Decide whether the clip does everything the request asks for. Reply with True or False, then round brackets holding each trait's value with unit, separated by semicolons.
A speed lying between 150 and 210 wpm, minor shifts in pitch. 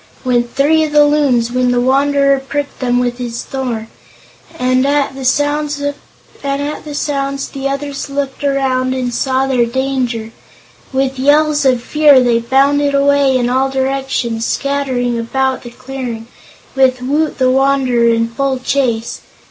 False (140 wpm; 2.1 semitones)